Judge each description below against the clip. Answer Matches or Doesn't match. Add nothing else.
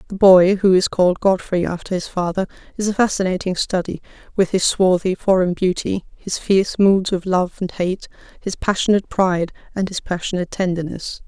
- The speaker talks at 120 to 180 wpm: Matches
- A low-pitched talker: Doesn't match